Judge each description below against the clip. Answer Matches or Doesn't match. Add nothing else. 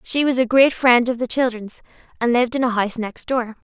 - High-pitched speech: Matches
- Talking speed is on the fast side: Matches